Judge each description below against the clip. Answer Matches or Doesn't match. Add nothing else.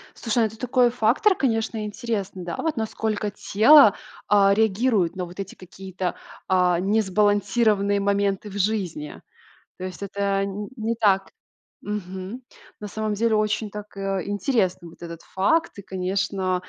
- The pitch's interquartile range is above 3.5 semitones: Doesn't match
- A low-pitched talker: Doesn't match